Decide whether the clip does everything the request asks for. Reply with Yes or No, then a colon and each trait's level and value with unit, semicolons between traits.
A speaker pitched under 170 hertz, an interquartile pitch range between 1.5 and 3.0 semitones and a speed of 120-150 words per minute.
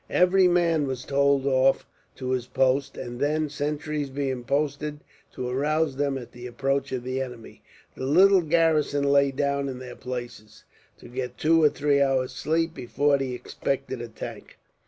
No: medium, 140 Hz; narrow, 2.6 semitones; average, 165 wpm